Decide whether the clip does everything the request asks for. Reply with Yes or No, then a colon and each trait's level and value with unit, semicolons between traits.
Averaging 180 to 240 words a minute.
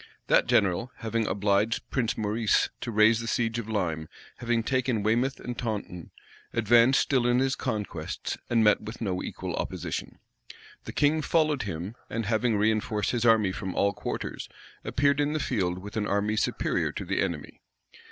No: average, 170 wpm